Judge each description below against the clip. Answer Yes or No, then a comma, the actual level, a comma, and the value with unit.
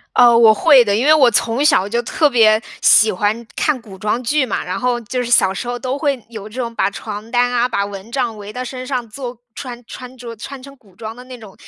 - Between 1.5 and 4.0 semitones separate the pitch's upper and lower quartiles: Yes, average, 2.9 semitones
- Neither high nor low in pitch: No, high, 240 Hz